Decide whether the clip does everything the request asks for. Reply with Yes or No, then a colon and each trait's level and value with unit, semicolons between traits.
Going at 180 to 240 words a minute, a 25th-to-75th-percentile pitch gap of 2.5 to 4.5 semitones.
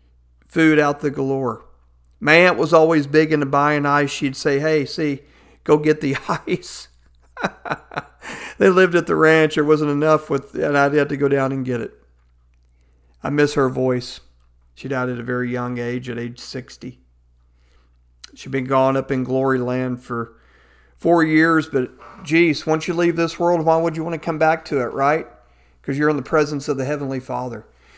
No: average, 190 wpm; average, 4.9 semitones